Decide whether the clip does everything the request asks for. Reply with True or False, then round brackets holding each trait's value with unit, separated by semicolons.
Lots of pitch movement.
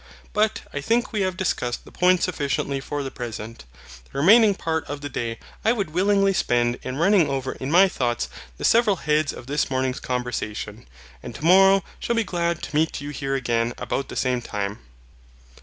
True (7.0 semitones)